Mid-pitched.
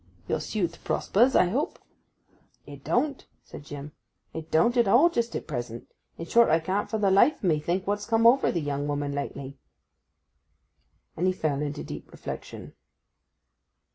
Yes: medium, 180 Hz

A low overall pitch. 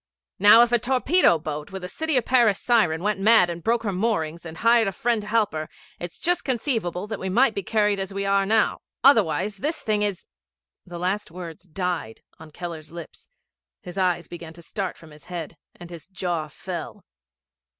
No: high, 195 Hz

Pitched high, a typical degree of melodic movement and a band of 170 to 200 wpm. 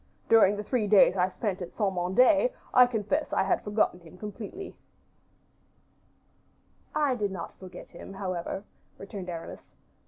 No: high, 200 Hz; average, 3.3 semitones; average, 145 wpm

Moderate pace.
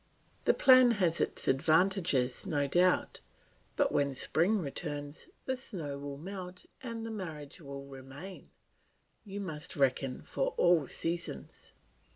No: slow, 130 wpm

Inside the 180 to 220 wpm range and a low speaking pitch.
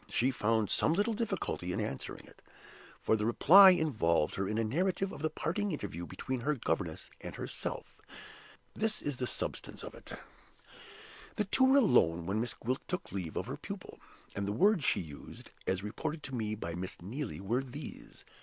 Yes: average, 185 wpm; low, 125 Hz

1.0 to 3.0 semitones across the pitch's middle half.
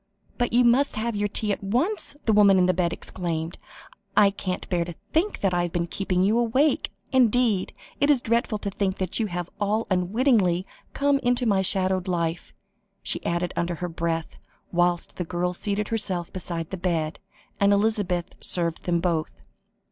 No: average, 4.2 semitones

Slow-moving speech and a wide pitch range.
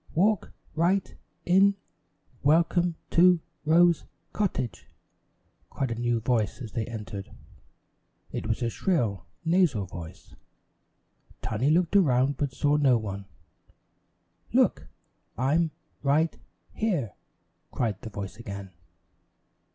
Yes: slow, 105 wpm; wide, 7.4 semitones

